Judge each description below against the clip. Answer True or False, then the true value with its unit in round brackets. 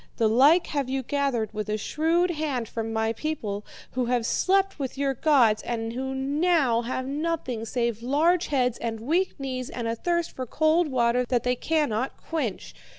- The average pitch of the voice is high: True (260 Hz)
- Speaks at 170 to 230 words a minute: True (180 wpm)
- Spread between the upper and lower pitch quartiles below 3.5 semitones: False (4.9 semitones)